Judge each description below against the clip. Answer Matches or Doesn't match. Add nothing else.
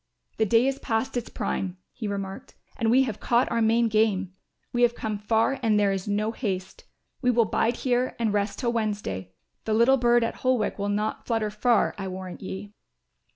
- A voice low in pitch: Doesn't match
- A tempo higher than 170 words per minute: Matches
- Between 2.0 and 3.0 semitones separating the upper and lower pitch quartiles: Matches